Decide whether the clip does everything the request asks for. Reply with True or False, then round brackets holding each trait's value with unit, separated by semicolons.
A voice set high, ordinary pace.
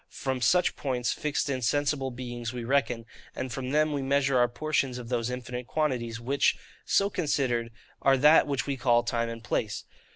False (130 Hz; 185 wpm)